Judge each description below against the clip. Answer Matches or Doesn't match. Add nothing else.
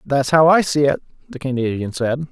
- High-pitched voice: Doesn't match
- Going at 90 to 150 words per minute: Doesn't match